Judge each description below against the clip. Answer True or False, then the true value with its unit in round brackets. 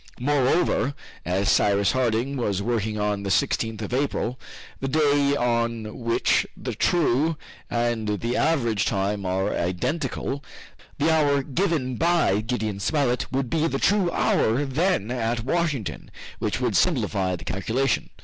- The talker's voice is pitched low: True (120 Hz)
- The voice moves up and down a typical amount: True (5.0 semitones)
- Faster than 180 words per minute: False (140 wpm)